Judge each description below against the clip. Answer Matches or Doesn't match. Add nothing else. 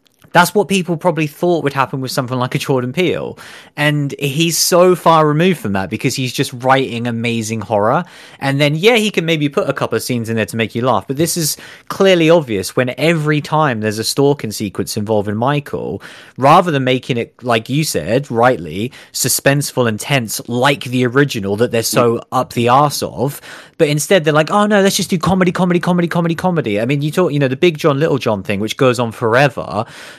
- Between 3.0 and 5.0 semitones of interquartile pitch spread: Doesn't match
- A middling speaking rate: Doesn't match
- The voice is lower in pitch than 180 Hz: Matches